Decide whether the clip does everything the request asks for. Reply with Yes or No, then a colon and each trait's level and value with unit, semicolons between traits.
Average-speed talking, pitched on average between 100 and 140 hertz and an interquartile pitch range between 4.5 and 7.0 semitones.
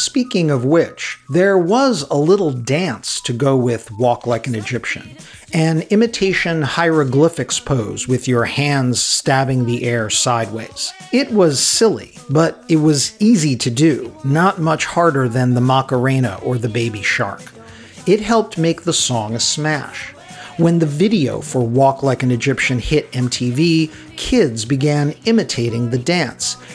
Yes: average, 150 wpm; low, 135 Hz; average, 5.2 semitones